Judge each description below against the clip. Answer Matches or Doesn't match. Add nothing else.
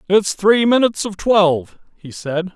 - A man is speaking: Matches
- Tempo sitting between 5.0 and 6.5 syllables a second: Doesn't match